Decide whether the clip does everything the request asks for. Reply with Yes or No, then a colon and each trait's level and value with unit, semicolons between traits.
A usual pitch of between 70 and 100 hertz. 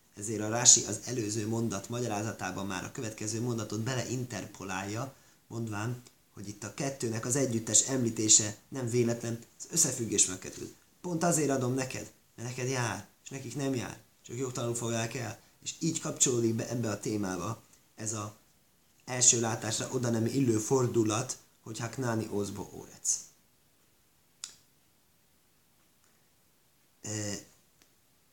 No: low, 115 Hz